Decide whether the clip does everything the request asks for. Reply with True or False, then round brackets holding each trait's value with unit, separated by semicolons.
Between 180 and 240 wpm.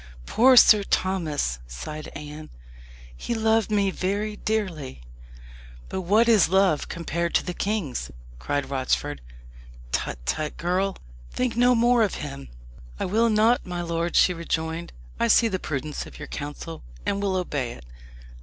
False (155 wpm)